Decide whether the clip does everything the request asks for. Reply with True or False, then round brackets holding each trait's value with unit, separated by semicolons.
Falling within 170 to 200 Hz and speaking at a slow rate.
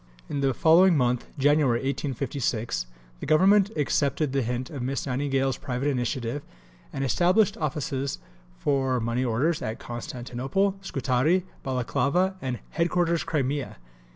False (135 Hz; 125 wpm)